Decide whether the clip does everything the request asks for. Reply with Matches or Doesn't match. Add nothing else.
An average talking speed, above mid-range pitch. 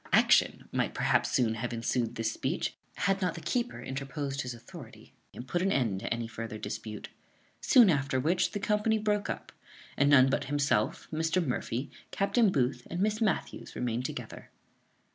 Doesn't match